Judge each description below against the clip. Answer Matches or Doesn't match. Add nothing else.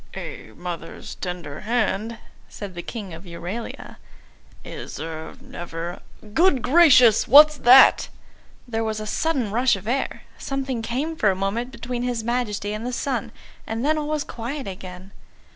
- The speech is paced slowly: Doesn't match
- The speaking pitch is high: Matches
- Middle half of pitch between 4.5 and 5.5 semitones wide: Matches